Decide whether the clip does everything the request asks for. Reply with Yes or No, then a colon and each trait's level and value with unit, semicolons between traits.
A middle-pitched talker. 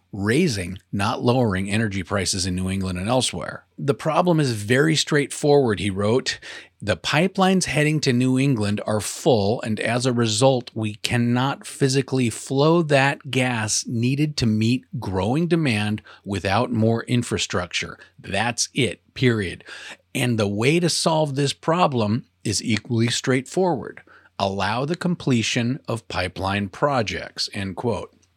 No: low, 120 Hz